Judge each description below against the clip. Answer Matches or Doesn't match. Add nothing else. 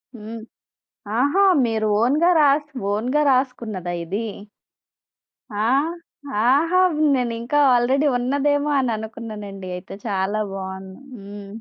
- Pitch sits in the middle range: Doesn't match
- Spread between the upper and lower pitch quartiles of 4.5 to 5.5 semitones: Matches